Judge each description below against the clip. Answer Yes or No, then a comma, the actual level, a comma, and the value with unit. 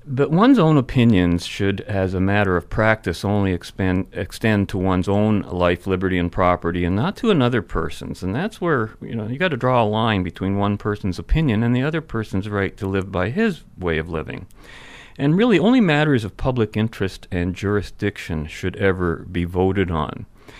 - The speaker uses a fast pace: No, average, 190 wpm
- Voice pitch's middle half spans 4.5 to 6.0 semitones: Yes, average, 4.8 semitones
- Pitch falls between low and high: No, low, 100 Hz